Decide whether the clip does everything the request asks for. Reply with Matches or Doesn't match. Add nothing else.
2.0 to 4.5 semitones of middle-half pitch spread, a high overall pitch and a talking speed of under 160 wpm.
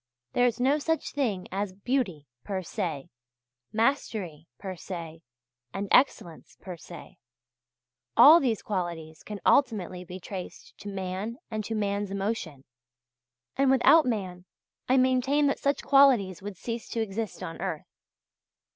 Doesn't match